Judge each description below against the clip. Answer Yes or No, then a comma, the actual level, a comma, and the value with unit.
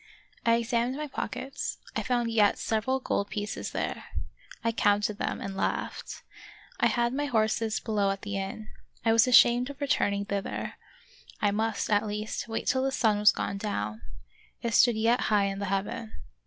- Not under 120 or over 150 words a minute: No, average, 180 wpm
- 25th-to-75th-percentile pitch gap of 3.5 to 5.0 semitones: No, average, 2.8 semitones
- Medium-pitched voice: No, high, 220 Hz